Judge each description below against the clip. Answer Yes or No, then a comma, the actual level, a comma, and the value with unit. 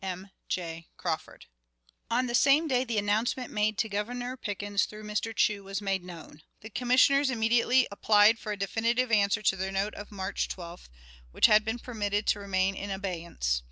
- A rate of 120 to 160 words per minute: No, average, 180 wpm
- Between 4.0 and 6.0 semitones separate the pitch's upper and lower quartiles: No, average, 3.3 semitones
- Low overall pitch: No, high, 210 Hz